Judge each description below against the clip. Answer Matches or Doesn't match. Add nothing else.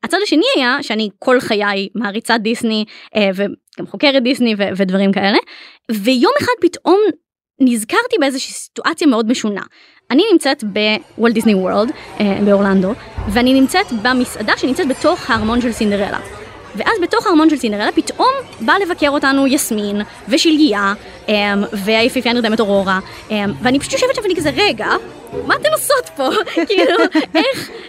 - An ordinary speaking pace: Matches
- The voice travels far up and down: Matches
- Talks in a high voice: Matches